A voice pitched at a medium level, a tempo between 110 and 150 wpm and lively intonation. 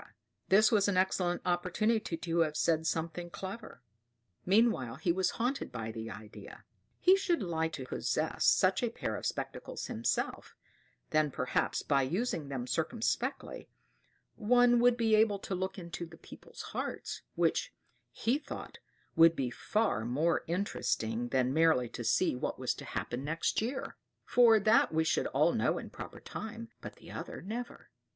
No: medium, 175 Hz; average, 160 wpm; wide, 7.2 semitones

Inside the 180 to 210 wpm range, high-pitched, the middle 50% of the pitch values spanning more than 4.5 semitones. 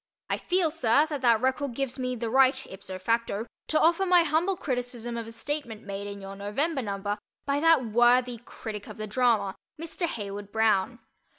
Yes: average, 185 wpm; high, 240 Hz; average, 5.1 semitones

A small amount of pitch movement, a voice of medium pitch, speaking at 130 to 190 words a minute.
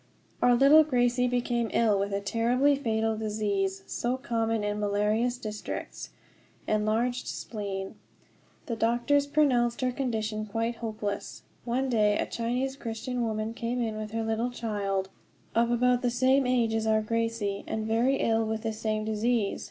No: narrow, 2.3 semitones; high, 230 Hz; average, 155 wpm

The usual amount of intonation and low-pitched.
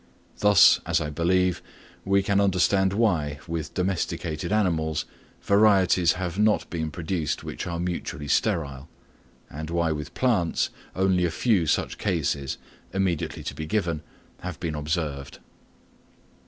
Yes: average, 3.6 semitones; very low, 85 Hz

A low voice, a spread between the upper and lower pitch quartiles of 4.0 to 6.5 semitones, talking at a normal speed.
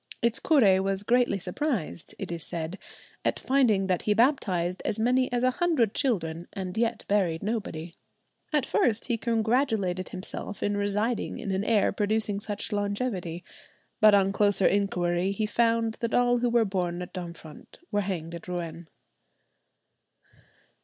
No: high, 205 Hz; average, 4.3 semitones; average, 155 wpm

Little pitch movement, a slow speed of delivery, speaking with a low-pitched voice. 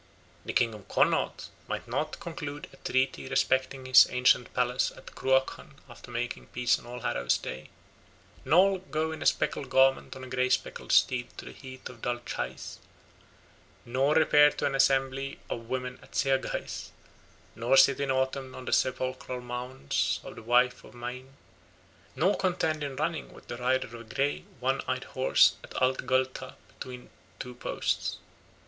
No: narrow, 1.8 semitones; average, 165 wpm; low, 130 Hz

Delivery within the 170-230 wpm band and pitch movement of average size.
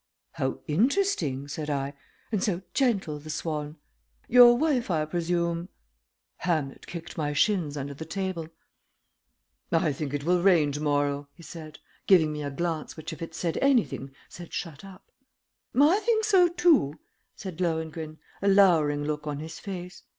No: average, 160 wpm; average, 4.5 semitones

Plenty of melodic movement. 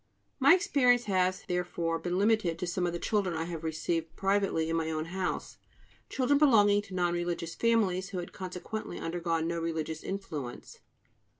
No: average, 3.6 semitones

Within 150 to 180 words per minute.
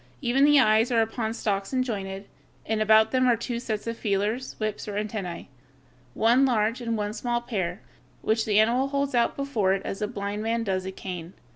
No: fast, 205 wpm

